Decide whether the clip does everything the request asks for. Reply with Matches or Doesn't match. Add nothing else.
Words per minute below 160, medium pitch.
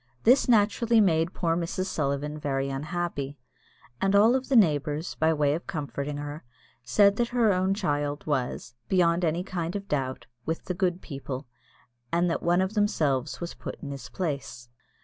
Doesn't match